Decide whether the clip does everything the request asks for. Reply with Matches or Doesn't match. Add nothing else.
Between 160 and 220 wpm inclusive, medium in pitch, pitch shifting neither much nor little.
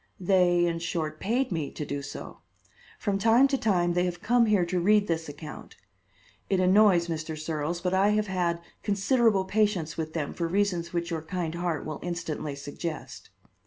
Matches